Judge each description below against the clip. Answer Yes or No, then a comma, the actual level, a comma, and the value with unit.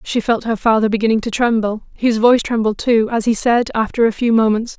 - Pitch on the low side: No, high, 225 Hz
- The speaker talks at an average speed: No, fast, 225 wpm